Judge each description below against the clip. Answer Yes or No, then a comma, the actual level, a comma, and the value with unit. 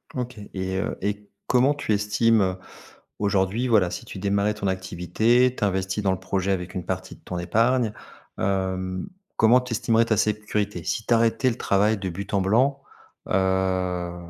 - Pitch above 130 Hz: No, low, 100 Hz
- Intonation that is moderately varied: Yes, average, 3.2 semitones